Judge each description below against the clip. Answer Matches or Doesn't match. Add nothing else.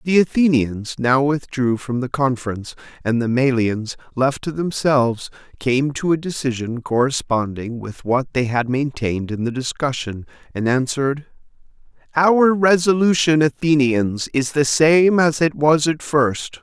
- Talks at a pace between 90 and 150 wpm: Matches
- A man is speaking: Matches